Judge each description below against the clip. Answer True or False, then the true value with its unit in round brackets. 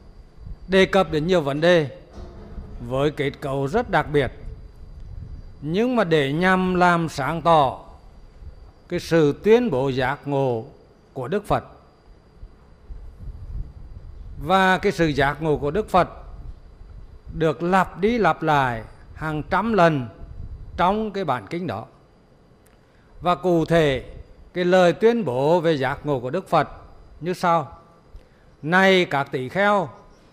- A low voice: False (145 Hz)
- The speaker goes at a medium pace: False (135 wpm)